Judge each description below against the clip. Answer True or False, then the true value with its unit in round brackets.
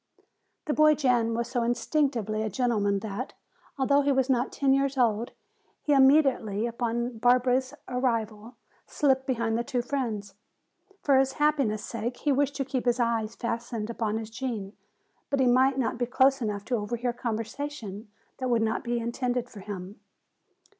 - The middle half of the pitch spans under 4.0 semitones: True (3.0 semitones)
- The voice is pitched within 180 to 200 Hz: False (245 Hz)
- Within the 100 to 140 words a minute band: False (165 wpm)